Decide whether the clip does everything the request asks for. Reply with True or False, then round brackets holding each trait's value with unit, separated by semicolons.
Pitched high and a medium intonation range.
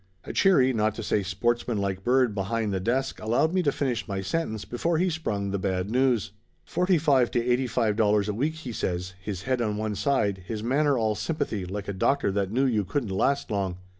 False (115 Hz; 4.9 semitones)